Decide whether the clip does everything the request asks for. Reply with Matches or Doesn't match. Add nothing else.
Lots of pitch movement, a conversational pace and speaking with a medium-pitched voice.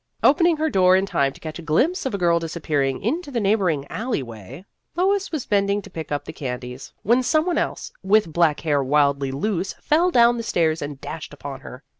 Doesn't match